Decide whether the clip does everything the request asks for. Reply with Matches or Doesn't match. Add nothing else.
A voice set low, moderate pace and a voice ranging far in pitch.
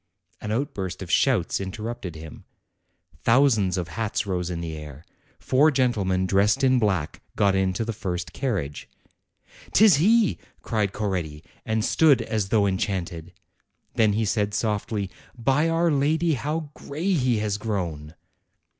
Matches